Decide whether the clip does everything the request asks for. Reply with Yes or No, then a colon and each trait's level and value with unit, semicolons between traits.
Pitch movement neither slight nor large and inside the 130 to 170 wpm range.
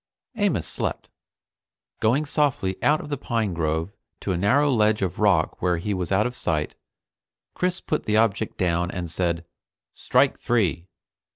No: wide, 5.8 semitones; average, 160 wpm